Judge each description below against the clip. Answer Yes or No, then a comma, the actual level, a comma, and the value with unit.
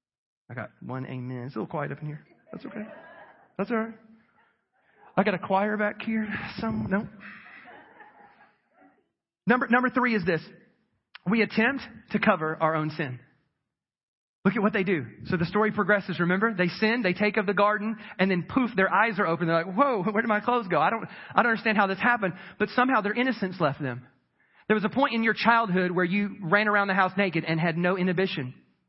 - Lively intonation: No, average, 4.1 semitones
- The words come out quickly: Yes, fast, 210 wpm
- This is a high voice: Yes, high, 205 Hz